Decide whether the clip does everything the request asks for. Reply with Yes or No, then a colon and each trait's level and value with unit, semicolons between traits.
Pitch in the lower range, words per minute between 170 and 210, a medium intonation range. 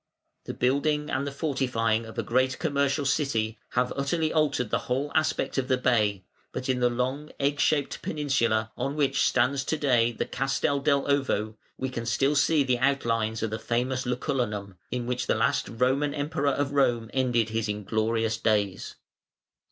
Yes: low, 130 Hz; average, 175 wpm; average, 3.6 semitones